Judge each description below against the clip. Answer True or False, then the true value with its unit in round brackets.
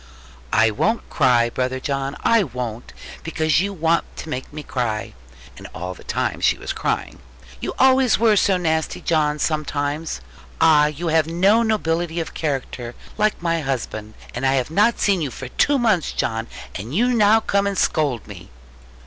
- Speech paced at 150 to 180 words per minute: True (175 wpm)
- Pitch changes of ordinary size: False (7.2 semitones)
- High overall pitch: False (155 Hz)